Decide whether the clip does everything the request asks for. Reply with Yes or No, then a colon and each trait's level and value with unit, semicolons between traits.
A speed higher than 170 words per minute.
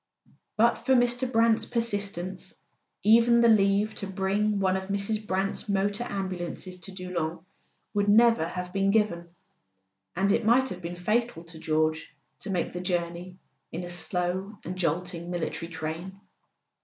No: average, 150 wpm